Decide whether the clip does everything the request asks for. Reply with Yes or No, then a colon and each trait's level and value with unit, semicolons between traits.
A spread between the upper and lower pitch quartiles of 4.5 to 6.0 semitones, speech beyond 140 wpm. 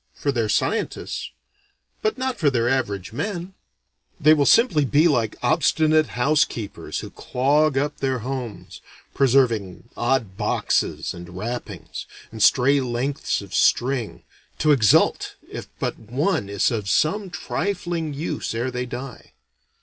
No: average, 4.8 semitones; slow, 135 wpm